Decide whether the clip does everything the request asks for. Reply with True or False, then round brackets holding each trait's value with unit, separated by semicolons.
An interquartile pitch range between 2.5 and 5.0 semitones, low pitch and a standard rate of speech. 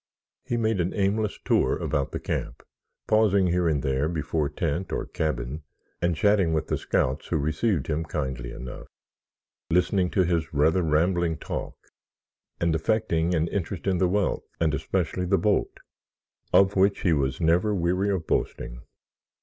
True (3.8 semitones; 85 Hz; 160 wpm)